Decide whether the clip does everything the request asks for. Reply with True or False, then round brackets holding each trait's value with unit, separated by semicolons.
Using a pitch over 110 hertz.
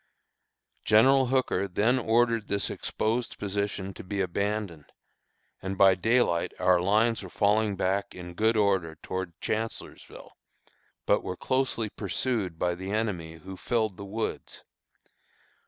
False (100 Hz)